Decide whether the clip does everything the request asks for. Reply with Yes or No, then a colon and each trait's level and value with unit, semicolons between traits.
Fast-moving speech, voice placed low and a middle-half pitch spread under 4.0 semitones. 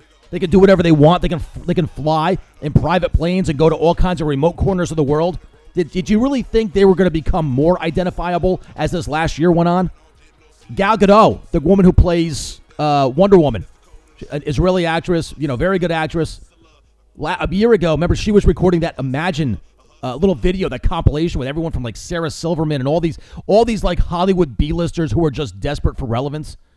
No: fast, 210 wpm; medium, 165 Hz; average, 3.3 semitones